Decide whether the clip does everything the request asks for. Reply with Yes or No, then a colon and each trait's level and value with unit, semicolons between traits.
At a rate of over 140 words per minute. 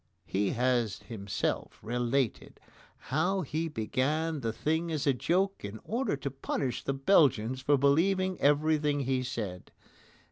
No: slow, 135 wpm